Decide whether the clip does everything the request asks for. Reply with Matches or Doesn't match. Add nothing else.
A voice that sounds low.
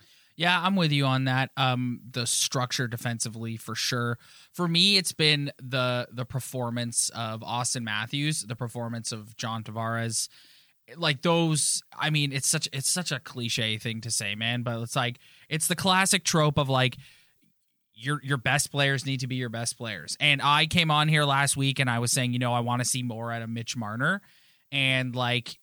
Matches